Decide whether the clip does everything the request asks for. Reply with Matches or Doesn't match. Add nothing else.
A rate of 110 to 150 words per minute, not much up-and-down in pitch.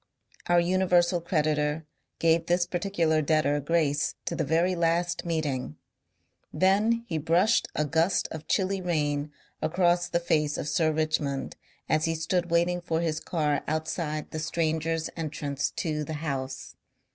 Matches